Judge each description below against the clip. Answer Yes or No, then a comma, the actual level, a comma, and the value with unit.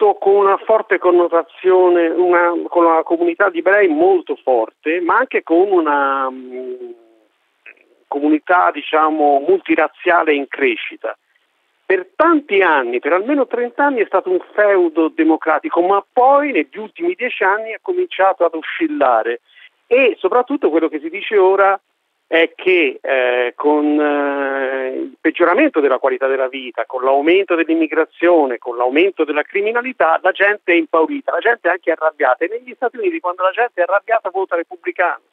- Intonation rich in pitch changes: Yes, wide, 7.5 semitones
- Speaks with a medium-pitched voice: Yes, medium, 180 Hz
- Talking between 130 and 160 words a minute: Yes, average, 150 wpm